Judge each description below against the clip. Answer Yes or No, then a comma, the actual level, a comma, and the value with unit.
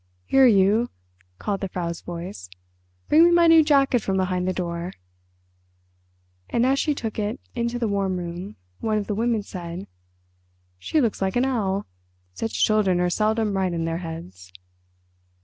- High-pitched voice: Yes, high, 200 Hz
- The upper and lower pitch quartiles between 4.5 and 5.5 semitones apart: Yes, average, 4.8 semitones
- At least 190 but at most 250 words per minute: No, average, 165 wpm